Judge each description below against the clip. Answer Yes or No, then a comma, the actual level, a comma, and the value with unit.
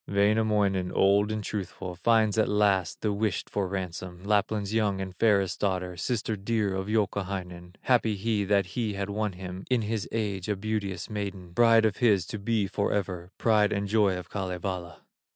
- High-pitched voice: No, low, 100 Hz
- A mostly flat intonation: Yes, narrow, 2.3 semitones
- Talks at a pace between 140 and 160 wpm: No, average, 170 wpm